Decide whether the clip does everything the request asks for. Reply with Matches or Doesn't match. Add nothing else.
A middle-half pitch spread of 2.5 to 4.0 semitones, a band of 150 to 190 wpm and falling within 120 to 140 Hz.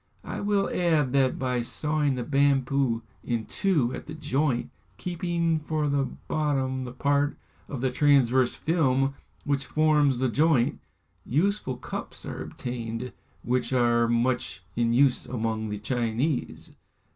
Doesn't match